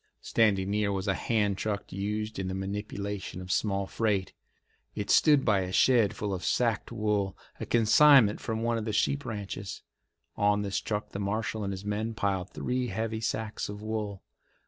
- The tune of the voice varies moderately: No, narrow, 2.0 semitones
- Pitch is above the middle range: No, low, 105 Hz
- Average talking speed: Yes, average, 180 wpm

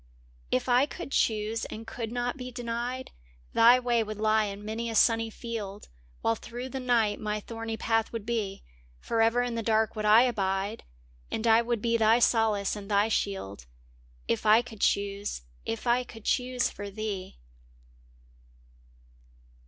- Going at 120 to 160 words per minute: No, average, 170 wpm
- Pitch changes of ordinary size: No, narrow, 2.3 semitones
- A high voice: Yes, high, 225 Hz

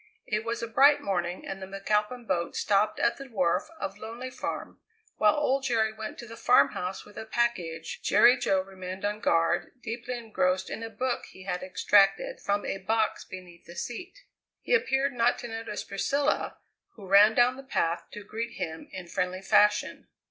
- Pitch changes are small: No, average, 4.1 semitones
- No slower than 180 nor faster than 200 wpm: Yes, average, 185 wpm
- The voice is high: Yes, high, 210 Hz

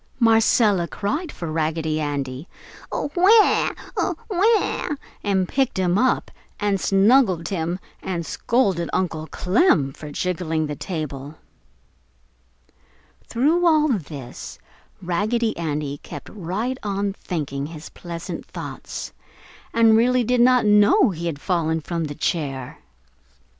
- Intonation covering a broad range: Yes, wide, 6.6 semitones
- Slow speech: Yes, slow, 115 wpm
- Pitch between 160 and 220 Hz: Yes, medium, 185 Hz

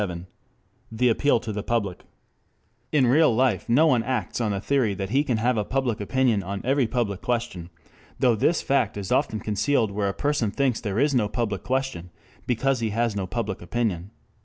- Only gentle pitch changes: No, average, 4.3 semitones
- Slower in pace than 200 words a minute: No, fast, 205 wpm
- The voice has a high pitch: No, low, 115 Hz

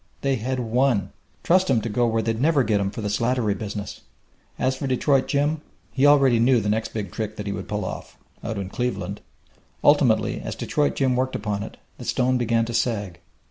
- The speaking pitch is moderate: No, low, 115 Hz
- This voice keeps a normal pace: No, fast, 210 wpm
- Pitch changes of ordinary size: Yes, average, 3.9 semitones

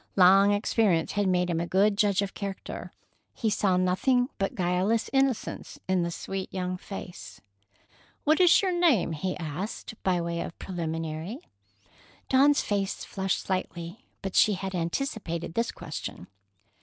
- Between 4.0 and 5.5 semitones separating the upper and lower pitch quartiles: No, average, 3.3 semitones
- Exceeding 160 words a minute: No, average, 145 wpm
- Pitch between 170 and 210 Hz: Yes, high, 190 Hz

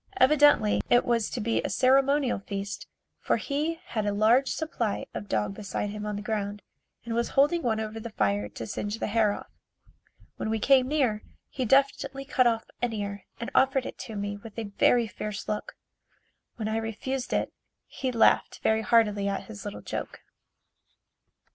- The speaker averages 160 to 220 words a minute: Yes, average, 180 wpm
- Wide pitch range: No, average, 3.9 semitones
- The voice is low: No, high, 225 Hz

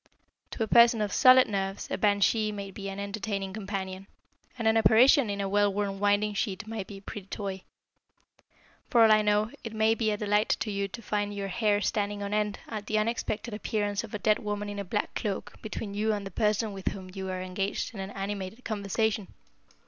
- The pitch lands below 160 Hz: No, high, 205 Hz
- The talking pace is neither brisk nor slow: No, fast, 210 wpm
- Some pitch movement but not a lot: No, narrow, 1.6 semitones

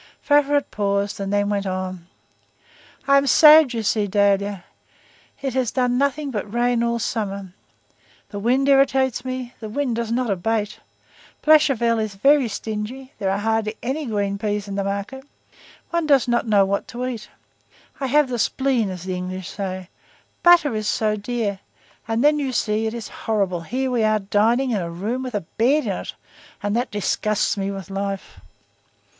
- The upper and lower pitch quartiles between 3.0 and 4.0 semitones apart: No, average, 4.4 semitones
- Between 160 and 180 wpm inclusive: Yes, average, 175 wpm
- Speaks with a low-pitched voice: No, high, 220 Hz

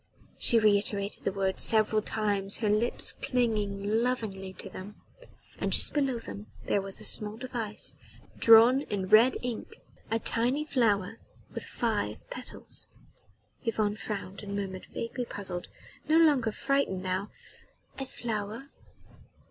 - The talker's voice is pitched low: No, high, 215 Hz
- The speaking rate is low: Yes, slow, 130 wpm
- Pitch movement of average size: Yes, average, 3.1 semitones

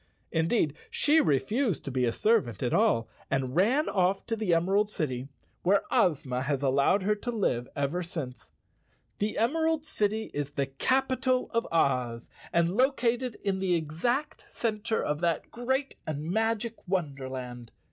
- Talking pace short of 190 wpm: Yes, average, 160 wpm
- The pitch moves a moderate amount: No, wide, 8.8 semitones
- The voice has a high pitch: No, medium, 180 Hz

